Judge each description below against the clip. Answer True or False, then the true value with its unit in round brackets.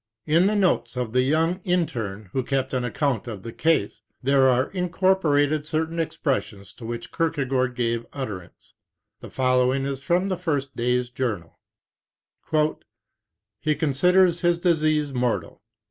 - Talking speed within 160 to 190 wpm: False (145 wpm)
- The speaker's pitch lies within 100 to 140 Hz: True (135 Hz)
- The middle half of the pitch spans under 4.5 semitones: False (5.0 semitones)